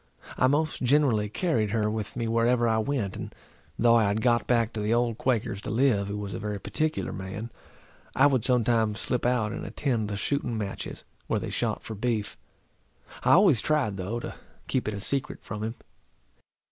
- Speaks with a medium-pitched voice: No, low, 115 Hz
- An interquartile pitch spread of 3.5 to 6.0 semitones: No, average, 3.0 semitones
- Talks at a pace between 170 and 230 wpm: Yes, average, 195 wpm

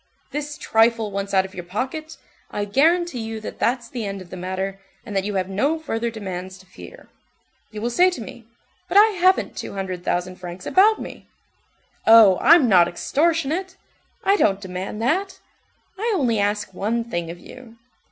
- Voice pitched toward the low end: No, high, 225 Hz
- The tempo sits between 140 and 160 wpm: No, average, 180 wpm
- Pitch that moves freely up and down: Yes, wide, 7.7 semitones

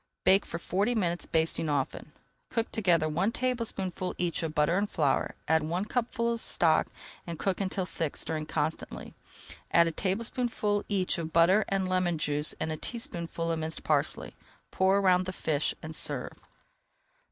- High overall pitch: No, medium, 180 Hz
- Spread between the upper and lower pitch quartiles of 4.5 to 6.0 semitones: No, average, 3.8 semitones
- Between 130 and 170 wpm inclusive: Yes, average, 165 wpm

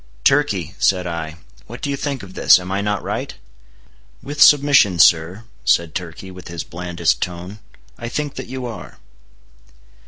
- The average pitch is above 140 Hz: No, very low, 95 Hz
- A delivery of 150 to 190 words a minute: Yes, average, 160 wpm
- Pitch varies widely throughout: Yes, wide, 6.8 semitones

